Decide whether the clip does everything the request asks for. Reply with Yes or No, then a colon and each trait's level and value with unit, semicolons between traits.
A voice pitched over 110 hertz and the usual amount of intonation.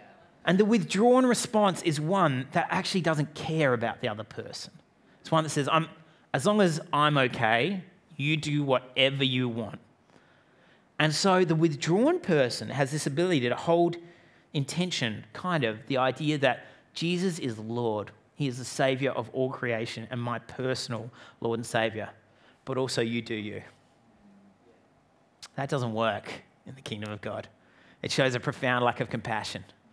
No: low, 135 Hz; wide, 5.7 semitones